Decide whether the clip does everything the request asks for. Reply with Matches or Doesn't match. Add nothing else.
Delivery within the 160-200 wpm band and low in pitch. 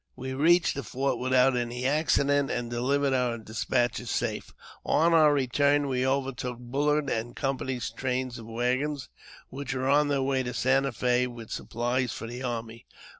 Matches